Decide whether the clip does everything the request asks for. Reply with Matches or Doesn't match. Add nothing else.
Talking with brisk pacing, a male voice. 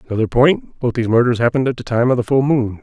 Matches